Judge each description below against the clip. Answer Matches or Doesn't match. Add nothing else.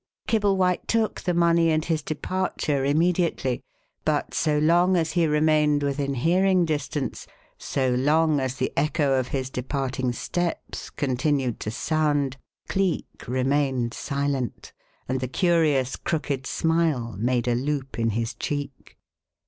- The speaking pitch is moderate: Matches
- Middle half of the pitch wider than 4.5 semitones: Doesn't match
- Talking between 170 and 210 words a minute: Doesn't match